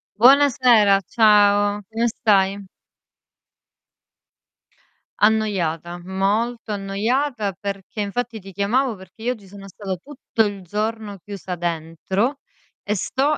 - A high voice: Yes, high, 205 Hz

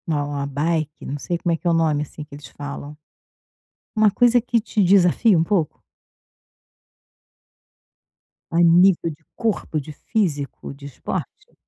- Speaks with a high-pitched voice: No, medium, 165 Hz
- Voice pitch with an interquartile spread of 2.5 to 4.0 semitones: No, average, 4.5 semitones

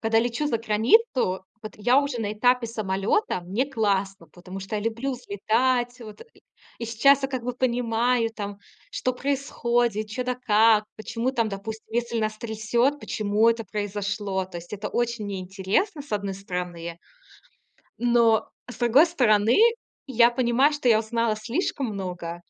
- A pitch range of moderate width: Yes, average, 3.1 semitones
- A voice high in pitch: Yes, high, 225 Hz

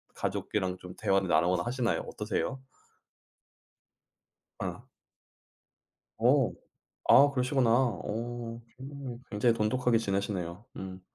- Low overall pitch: Yes, low, 115 Hz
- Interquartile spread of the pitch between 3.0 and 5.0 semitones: Yes, average, 4.6 semitones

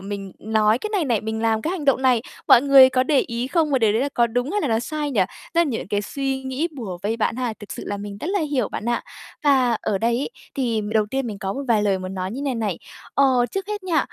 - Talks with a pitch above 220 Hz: Yes, high, 245 Hz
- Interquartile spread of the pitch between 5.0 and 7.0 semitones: No, average, 4.4 semitones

